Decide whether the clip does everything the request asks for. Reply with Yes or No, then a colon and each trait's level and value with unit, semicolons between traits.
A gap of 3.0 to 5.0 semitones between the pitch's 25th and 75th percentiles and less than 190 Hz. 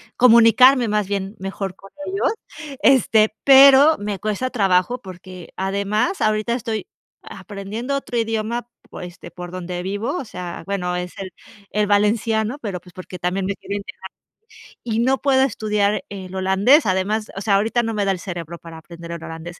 No: average, 3.6 semitones; high, 205 Hz